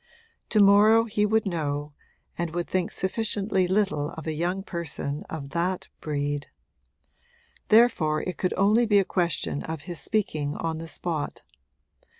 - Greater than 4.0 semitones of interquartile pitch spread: Yes, average, 4.8 semitones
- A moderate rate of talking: Yes, average, 150 wpm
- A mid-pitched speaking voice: Yes, medium, 175 Hz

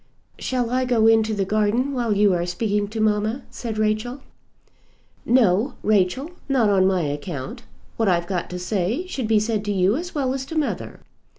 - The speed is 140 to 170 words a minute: No, average, 185 wpm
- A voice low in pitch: No, high, 215 Hz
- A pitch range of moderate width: Yes, average, 4.2 semitones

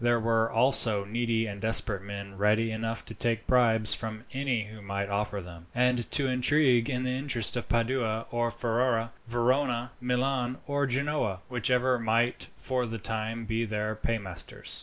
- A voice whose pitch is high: No, low, 115 Hz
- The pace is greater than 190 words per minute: No, average, 160 wpm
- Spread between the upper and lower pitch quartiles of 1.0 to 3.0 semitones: Yes, narrow, 2.5 semitones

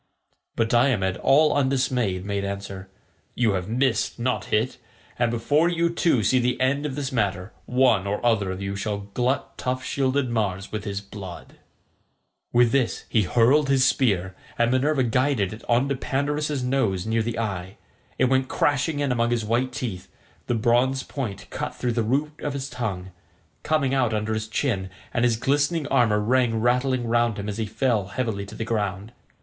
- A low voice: Yes, low, 120 Hz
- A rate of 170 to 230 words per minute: Yes, average, 180 wpm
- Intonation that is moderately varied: Yes, average, 4.1 semitones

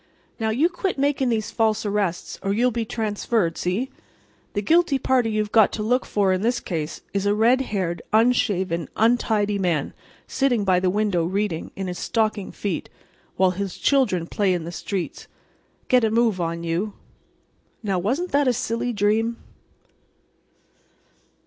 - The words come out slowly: No, average, 155 wpm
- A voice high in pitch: Yes, high, 210 Hz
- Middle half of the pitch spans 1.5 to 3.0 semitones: No, average, 4.0 semitones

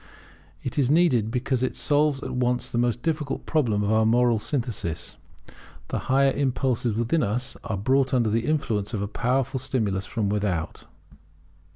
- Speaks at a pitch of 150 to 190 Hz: No, low, 125 Hz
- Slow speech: No, average, 165 wpm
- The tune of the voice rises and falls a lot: No, average, 3.7 semitones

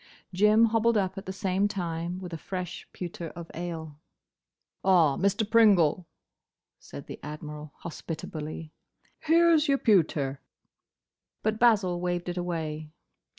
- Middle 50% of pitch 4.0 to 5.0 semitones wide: Yes, average, 4.4 semitones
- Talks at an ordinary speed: No, slow, 130 wpm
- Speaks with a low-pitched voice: No, medium, 180 Hz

